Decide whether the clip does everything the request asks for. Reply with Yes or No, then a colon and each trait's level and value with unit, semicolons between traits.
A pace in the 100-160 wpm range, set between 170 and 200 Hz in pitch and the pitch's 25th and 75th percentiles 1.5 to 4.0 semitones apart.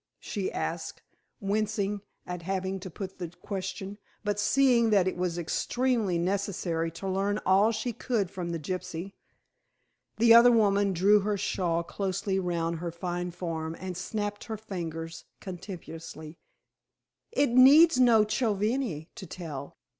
Yes: average, 140 wpm; high, 190 Hz; average, 3.5 semitones